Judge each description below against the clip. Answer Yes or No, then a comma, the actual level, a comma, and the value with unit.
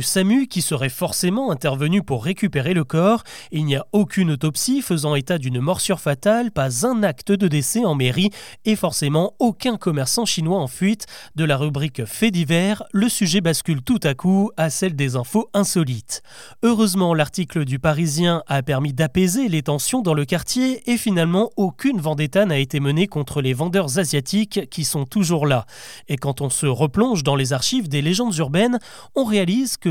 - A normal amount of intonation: No, wide, 5.7 semitones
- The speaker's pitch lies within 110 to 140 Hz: No, medium, 175 Hz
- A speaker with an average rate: Yes, average, 180 wpm